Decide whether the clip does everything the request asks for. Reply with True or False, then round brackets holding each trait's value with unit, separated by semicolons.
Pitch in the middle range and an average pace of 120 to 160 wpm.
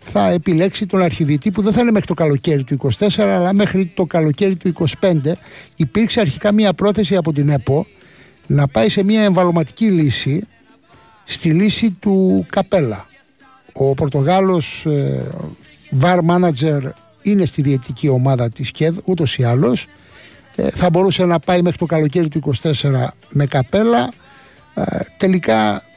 True (170 Hz; 150 wpm)